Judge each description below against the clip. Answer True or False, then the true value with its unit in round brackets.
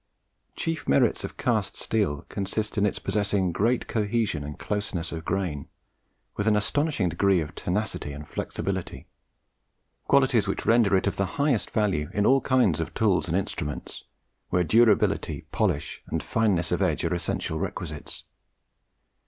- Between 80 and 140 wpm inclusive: False (150 wpm)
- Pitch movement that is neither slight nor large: True (4.5 semitones)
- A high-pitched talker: False (100 Hz)